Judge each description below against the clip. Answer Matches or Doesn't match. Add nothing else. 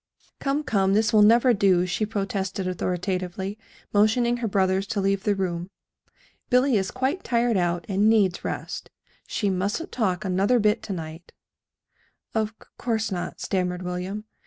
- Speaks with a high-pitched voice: Matches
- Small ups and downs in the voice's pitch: Doesn't match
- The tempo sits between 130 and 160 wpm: Matches